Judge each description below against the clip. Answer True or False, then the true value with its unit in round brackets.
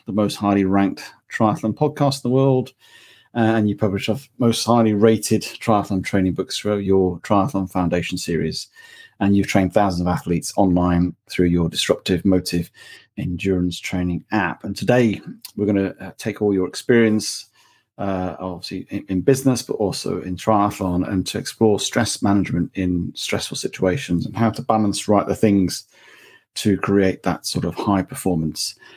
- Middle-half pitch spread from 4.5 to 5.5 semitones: False (3.2 semitones)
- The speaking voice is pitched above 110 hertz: False (100 Hz)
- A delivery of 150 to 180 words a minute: True (165 wpm)